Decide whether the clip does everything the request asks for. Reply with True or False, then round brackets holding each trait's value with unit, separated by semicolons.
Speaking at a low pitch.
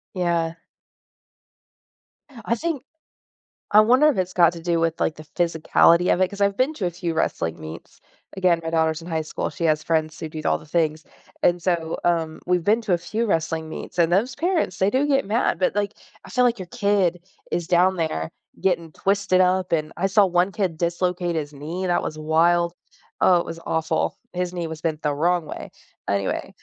False (175 Hz)